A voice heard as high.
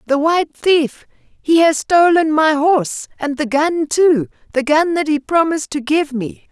Yes: very high, 300 Hz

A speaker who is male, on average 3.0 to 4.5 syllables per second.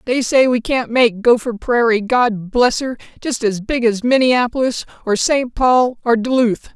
No: female; 4.3 syllables/s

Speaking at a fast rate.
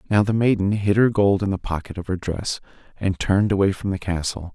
Yes: fast, 240 wpm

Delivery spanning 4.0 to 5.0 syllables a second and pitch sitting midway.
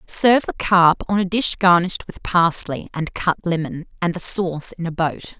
Yes: 4.9 syllables/s; medium, 175 Hz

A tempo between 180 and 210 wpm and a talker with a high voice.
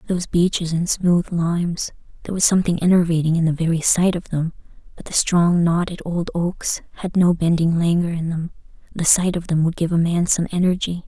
No: average, 190 wpm; medium, 170 Hz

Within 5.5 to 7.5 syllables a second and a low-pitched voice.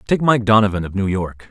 Yes: 5.8 syllables/s; low, 105 Hz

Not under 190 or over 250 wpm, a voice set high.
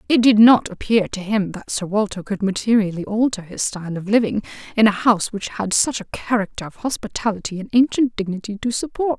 Yes: average, 200 wpm; high, 215 Hz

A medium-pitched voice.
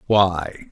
No: very low, 90 Hz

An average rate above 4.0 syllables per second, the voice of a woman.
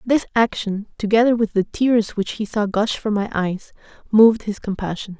Yes: 4.9 syllables/s; female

